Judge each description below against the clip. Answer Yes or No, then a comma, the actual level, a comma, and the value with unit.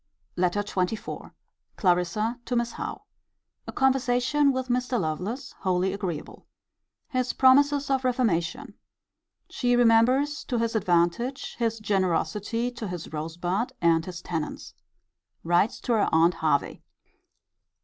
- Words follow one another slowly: Yes, slow, 120 wpm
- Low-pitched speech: No, high, 220 Hz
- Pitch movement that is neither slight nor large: No, wide, 6.0 semitones